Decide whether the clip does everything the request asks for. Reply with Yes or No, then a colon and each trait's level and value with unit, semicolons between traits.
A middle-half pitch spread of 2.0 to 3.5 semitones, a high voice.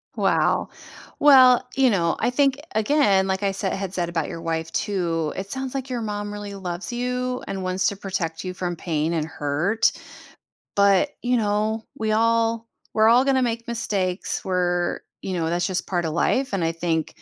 No: average, 4.8 semitones; high, 195 Hz